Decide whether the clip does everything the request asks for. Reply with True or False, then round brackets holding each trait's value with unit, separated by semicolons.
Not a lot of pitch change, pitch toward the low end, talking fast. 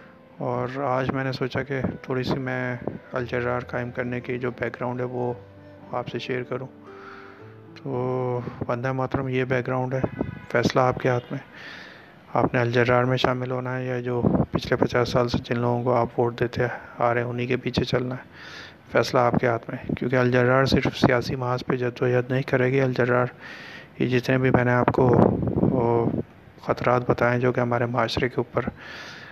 True (0.9 semitones; 125 Hz; 195 wpm)